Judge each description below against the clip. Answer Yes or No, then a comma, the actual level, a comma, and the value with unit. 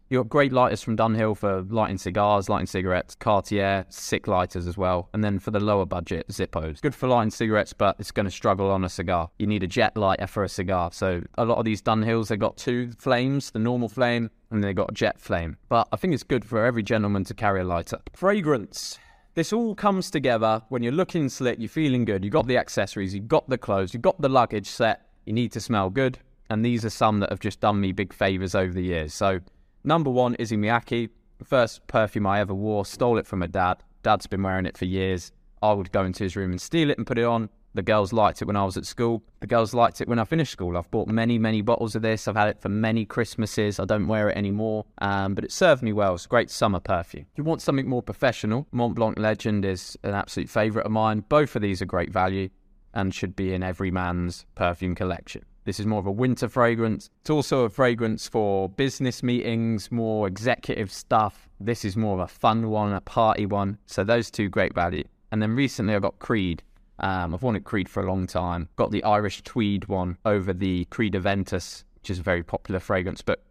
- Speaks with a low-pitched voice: Yes, low, 105 Hz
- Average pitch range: Yes, average, 3.4 semitones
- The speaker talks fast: Yes, fast, 235 wpm